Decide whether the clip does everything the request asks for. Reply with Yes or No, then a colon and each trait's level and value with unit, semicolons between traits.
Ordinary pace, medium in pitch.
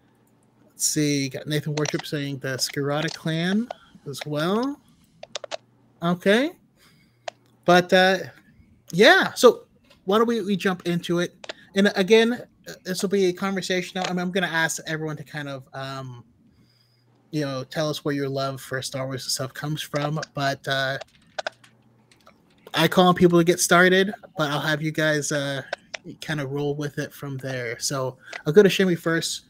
Yes: average, 165 wpm; medium, 155 Hz